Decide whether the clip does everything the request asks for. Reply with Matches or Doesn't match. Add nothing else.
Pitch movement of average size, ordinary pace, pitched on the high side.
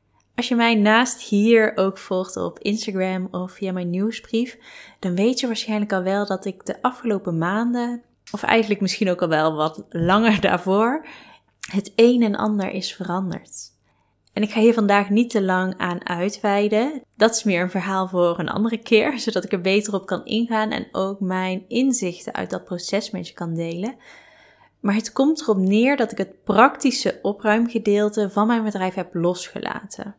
Matches